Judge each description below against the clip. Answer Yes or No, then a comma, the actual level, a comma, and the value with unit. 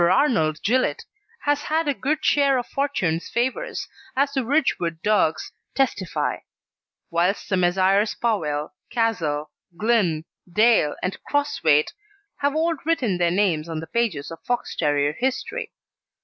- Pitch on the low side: No, high, 210 Hz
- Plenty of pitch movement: Yes, wide, 8.9 semitones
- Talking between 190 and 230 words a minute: No, slow, 135 wpm